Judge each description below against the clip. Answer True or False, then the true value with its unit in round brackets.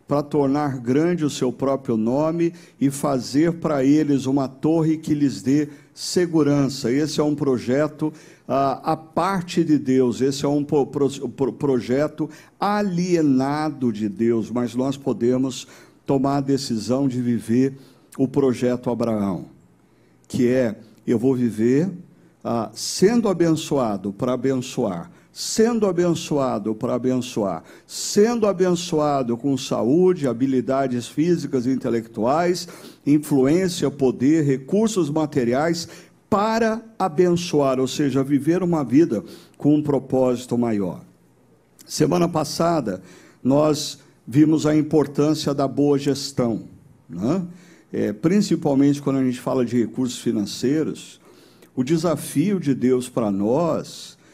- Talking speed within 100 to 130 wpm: True (120 wpm)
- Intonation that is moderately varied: True (3.7 semitones)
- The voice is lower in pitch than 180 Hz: True (140 Hz)